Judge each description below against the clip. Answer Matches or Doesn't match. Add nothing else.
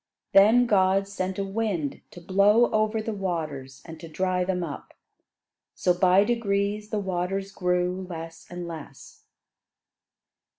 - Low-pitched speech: Doesn't match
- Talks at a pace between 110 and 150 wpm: Matches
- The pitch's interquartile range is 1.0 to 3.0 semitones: Matches